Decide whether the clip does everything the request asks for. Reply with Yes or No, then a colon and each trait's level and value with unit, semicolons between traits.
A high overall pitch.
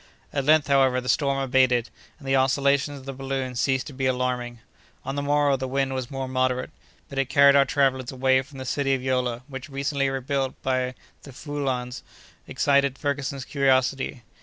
No: low, 135 Hz